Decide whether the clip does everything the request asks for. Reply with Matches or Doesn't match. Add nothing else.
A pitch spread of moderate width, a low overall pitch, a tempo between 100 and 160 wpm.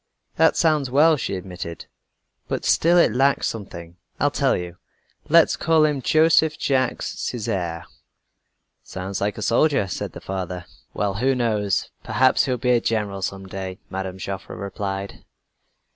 Doesn't match